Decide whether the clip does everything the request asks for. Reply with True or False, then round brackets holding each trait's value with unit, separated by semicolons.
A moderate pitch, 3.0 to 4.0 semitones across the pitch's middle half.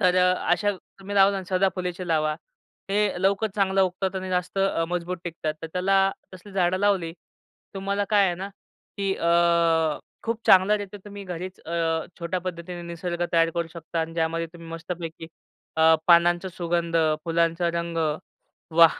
False (180 Hz; 2.4 semitones)